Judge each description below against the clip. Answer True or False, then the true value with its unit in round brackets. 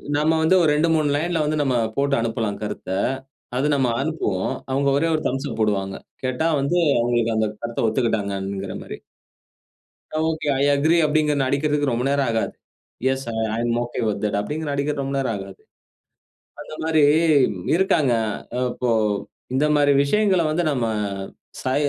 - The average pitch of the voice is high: False (140 Hz)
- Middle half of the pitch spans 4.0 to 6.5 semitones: True (4.6 semitones)